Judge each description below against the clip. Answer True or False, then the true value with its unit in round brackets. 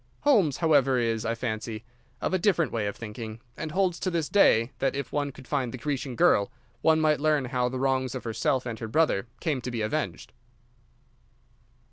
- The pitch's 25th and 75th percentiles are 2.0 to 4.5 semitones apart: False (5.0 semitones)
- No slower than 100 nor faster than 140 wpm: False (195 wpm)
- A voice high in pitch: False (130 Hz)